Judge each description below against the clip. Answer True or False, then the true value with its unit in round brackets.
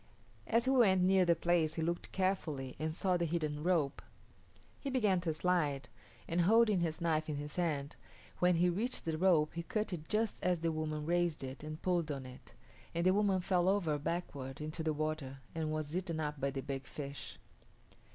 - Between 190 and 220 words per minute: True (200 wpm)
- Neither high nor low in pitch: True (165 Hz)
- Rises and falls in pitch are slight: False (3.2 semitones)